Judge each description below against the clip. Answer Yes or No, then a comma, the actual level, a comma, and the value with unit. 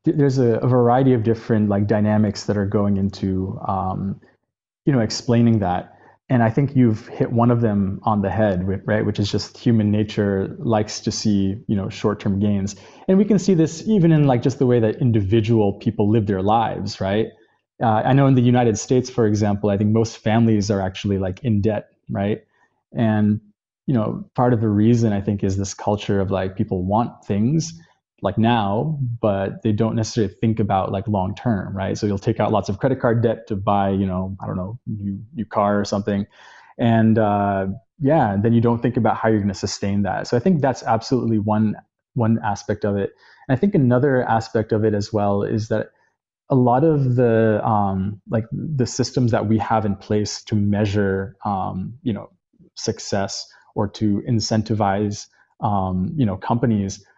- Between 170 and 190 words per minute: No, average, 200 wpm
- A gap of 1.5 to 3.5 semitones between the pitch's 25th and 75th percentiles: Yes, average, 2.7 semitones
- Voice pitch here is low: Yes, low, 110 Hz